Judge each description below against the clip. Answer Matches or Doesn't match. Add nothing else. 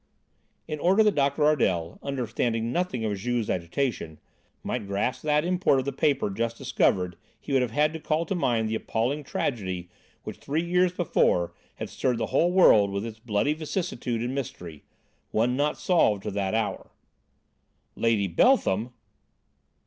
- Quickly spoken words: Doesn't match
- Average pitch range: Doesn't match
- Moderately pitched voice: Doesn't match